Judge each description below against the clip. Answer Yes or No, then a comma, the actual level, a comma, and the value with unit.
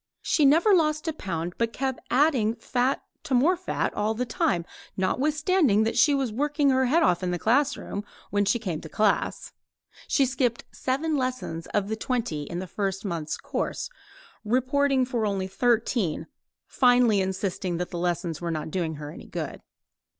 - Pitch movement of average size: No, wide, 6.4 semitones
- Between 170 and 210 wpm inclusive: Yes, average, 175 wpm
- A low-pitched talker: No, high, 230 Hz